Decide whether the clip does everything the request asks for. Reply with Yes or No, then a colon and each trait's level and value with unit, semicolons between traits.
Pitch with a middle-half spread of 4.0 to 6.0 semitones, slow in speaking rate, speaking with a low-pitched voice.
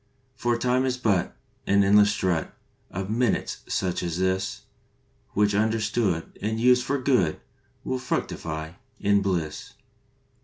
Yes: average, 4.4 semitones; slow, 125 wpm; low, 105 Hz